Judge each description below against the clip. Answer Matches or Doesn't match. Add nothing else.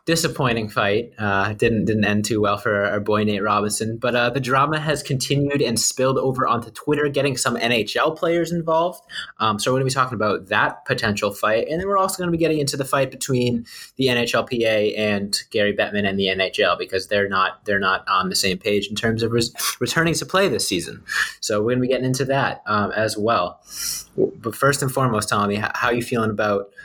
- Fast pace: Matches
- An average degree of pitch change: Matches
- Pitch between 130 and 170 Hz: Doesn't match